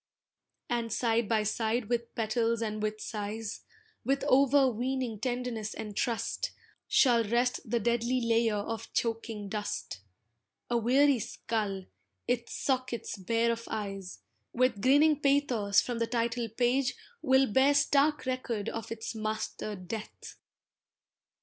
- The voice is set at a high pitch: Yes, high, 230 Hz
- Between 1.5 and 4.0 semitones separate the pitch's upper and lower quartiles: Yes, average, 2.7 semitones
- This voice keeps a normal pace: No, slow, 125 wpm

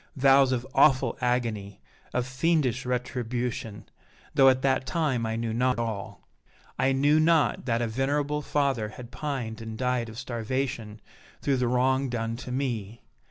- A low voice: Yes, low, 125 Hz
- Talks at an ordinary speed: Yes, average, 155 wpm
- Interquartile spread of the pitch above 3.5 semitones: No, average, 2.7 semitones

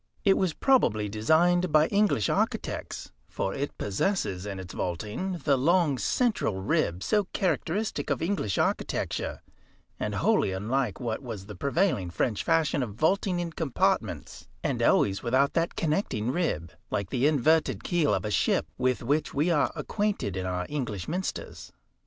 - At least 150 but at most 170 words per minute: Yes, average, 155 wpm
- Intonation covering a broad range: Yes, wide, 8.9 semitones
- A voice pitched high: No, medium, 140 Hz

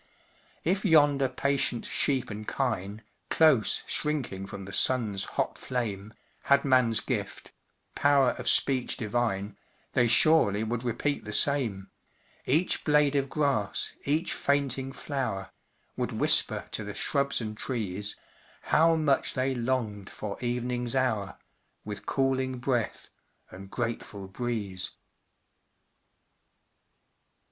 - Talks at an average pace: No, slow, 115 wpm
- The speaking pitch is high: No, low, 125 Hz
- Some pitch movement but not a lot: Yes, average, 4.6 semitones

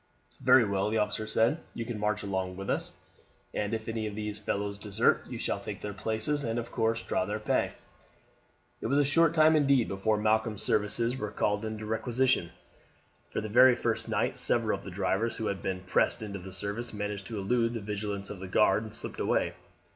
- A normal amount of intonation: No, narrow, 2.2 semitones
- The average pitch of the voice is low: Yes, low, 110 Hz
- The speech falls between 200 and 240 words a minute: Yes, fast, 205 wpm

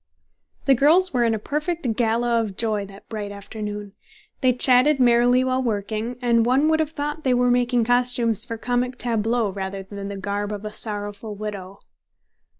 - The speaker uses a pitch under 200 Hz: No, high, 230 Hz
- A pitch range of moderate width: Yes, average, 3.3 semitones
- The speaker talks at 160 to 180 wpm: Yes, average, 175 wpm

